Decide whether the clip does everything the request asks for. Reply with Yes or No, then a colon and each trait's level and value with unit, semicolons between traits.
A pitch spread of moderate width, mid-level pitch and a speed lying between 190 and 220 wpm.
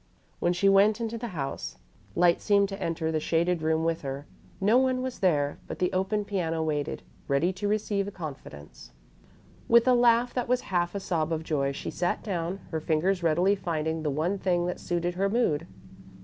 Yes: average, 4.0 semitones; medium, 175 Hz; average, 195 wpm